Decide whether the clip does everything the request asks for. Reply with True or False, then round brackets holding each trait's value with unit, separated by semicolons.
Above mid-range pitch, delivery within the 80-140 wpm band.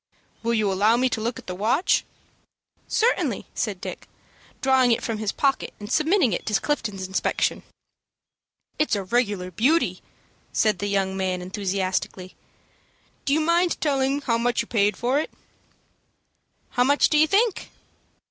False (230 Hz; 155 wpm)